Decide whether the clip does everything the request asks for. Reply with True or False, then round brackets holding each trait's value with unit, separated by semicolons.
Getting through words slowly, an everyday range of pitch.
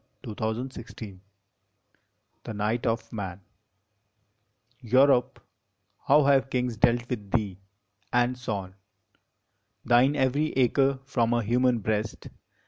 True (115 wpm; 3.0 semitones)